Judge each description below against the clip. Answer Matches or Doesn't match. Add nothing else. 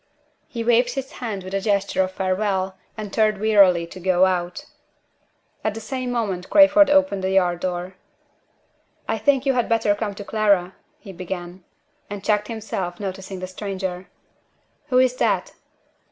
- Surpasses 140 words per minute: Matches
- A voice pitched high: Matches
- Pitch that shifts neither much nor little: Matches